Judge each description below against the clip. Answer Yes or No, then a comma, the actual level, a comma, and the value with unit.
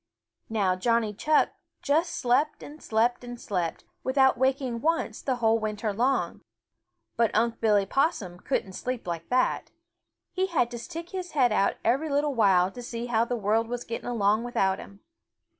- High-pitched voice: Yes, high, 235 Hz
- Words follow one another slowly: No, average, 170 wpm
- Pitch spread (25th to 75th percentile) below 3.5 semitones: No, average, 4.0 semitones